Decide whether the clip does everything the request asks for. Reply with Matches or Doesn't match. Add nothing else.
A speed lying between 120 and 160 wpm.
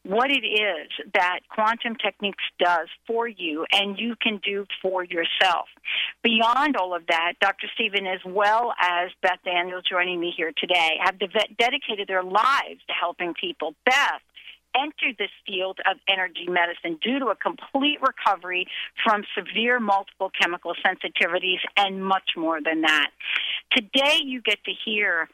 Matches